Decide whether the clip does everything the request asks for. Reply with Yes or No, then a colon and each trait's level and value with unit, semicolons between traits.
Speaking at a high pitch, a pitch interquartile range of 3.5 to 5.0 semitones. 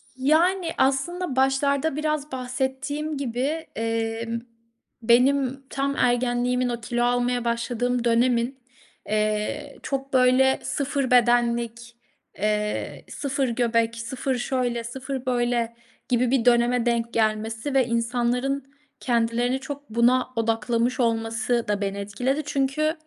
No: high, 245 Hz; narrow, 2.4 semitones